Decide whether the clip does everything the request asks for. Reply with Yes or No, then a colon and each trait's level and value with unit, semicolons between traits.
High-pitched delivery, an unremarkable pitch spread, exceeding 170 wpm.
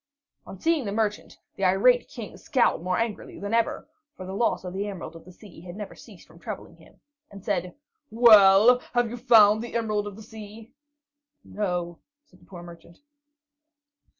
Yes: high, 205 Hz; average, 3.5 semitones; average, 180 wpm